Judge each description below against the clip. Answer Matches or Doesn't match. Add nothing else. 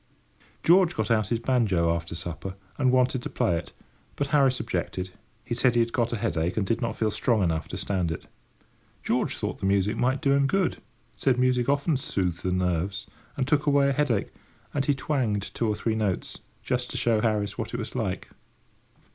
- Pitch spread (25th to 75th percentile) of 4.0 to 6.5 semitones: Matches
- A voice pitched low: Matches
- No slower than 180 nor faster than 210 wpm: Matches